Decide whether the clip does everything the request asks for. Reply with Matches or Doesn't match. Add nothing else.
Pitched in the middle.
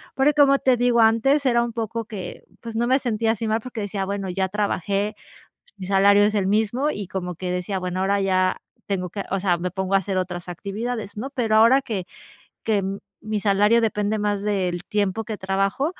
Doesn't match